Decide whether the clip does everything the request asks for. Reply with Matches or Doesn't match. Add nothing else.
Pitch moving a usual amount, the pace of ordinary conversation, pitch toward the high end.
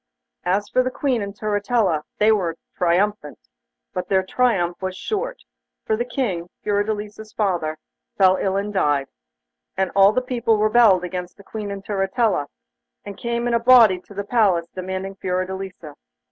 Matches